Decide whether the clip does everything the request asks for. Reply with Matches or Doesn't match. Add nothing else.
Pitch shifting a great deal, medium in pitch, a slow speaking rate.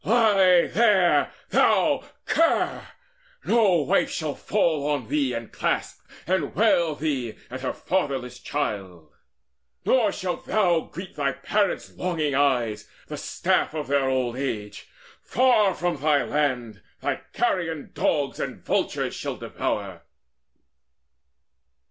Matches